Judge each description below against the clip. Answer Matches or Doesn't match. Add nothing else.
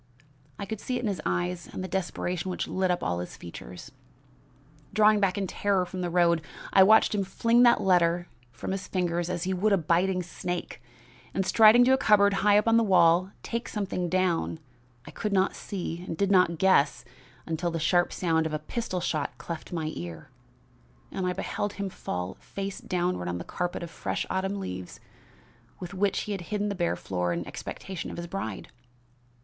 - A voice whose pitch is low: Doesn't match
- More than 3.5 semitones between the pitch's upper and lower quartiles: Doesn't match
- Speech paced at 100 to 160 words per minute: Doesn't match